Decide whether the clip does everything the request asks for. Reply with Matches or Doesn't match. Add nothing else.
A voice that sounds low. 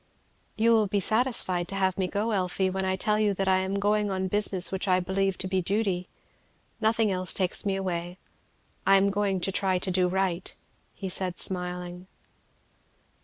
Doesn't match